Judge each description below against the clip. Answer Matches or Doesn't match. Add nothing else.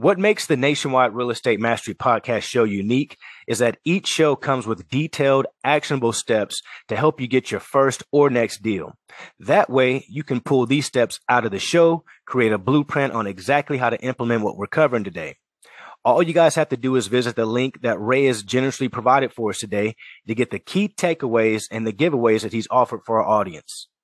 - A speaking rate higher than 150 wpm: Matches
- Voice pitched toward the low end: Matches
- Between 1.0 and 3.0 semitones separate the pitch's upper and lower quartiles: Doesn't match